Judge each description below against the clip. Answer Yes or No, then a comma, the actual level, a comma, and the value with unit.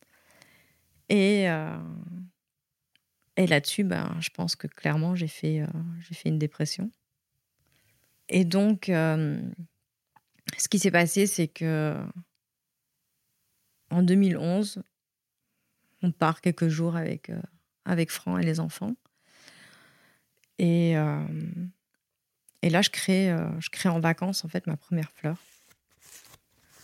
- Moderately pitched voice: Yes, medium, 170 Hz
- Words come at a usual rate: No, slow, 120 wpm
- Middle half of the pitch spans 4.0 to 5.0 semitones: No, average, 2.7 semitones